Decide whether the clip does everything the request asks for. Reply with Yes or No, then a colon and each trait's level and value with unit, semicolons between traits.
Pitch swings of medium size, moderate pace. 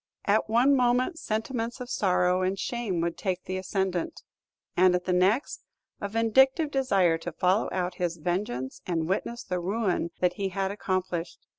Yes: average, 4.1 semitones; average, 165 wpm